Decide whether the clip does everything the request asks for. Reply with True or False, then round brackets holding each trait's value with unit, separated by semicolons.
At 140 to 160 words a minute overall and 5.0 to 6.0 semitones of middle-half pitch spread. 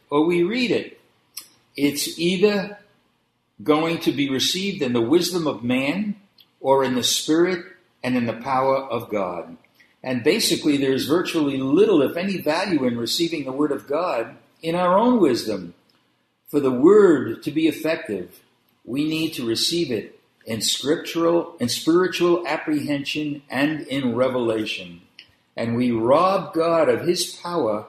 True (150 wpm; 5.5 semitones)